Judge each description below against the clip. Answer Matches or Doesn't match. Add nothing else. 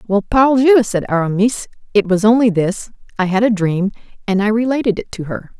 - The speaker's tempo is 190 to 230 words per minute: Matches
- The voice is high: Matches